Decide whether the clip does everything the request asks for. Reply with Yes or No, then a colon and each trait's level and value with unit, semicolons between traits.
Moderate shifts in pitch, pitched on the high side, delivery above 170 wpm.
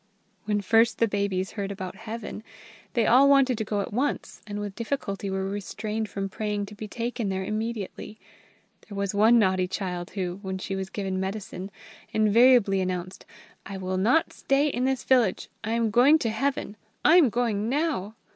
Yes: average, 3.4 semitones; high, 210 Hz; average, 180 wpm